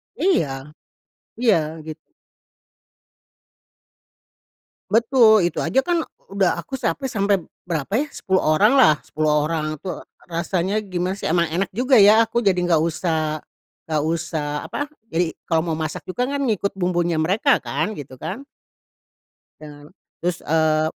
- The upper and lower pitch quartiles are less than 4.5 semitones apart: No, average, 5.2 semitones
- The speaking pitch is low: No, medium, 175 Hz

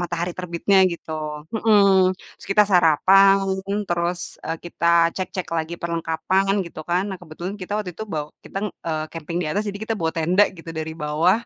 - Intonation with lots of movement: No, average, 3.0 semitones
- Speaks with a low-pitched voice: No, medium, 175 Hz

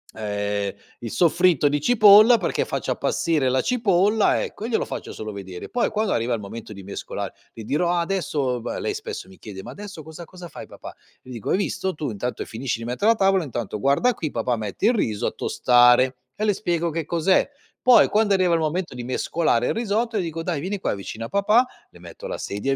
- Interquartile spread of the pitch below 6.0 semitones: No, wide, 8.8 semitones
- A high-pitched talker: No, medium, 165 Hz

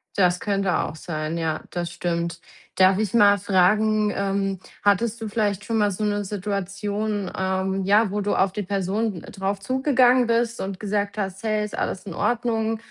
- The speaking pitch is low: No, high, 200 Hz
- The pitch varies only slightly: Yes, narrow, 2.1 semitones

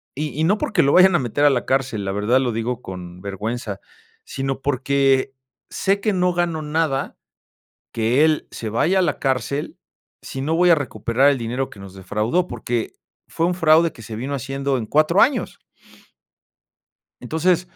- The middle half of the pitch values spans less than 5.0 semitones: No, wide, 5.5 semitones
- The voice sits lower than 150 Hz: Yes, low, 135 Hz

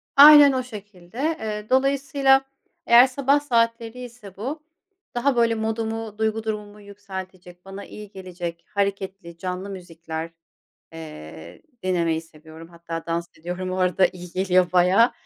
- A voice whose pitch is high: Yes, high, 195 Hz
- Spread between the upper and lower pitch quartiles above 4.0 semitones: Yes, average, 4.6 semitones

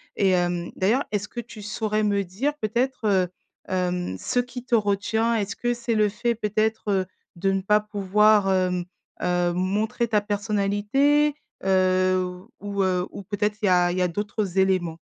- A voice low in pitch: No, high, 205 Hz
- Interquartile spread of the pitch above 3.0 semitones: No, average, 2.7 semitones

